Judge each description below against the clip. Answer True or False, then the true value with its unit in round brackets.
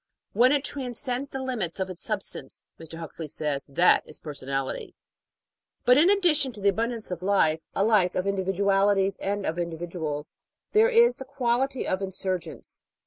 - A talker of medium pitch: False (195 Hz)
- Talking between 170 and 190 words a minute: False (160 wpm)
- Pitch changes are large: True (6.7 semitones)